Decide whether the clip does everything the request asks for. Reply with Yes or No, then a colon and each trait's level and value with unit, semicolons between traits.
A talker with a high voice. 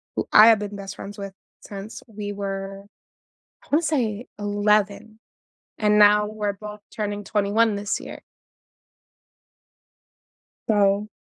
Yes: high, 205 Hz